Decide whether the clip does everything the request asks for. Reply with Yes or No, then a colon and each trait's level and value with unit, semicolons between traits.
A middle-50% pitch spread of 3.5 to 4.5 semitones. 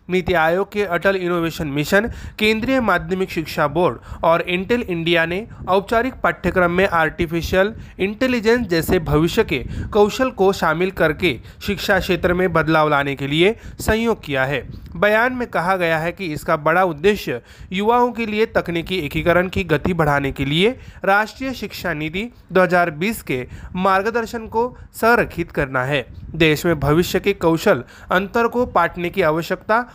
Yes: average, 4.2 semitones